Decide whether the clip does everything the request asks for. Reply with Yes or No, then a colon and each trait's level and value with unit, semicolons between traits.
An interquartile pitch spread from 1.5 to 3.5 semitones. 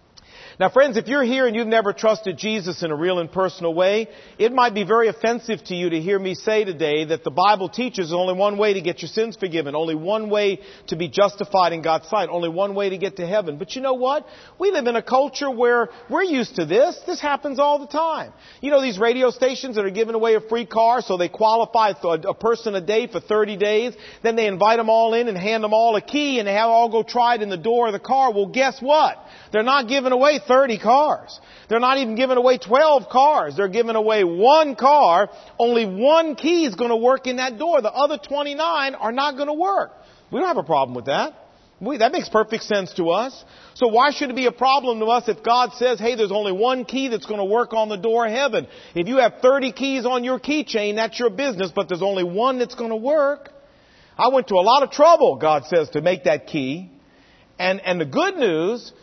No: average, 4.6 semitones